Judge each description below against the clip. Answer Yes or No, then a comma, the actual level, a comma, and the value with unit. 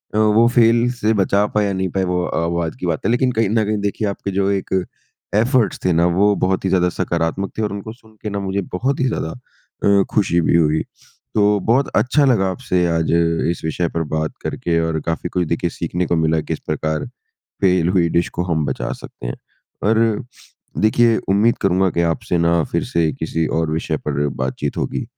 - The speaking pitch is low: Yes, very low, 95 Hz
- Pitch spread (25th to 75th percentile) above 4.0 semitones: Yes, average, 4.4 semitones